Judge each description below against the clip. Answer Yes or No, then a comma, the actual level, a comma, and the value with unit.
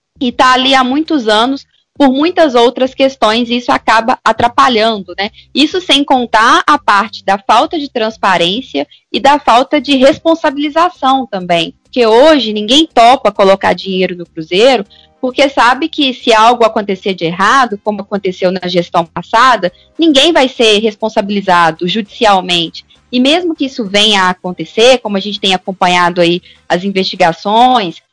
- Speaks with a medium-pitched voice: No, high, 225 Hz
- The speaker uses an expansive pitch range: Yes, wide, 5.9 semitones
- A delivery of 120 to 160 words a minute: Yes, average, 150 wpm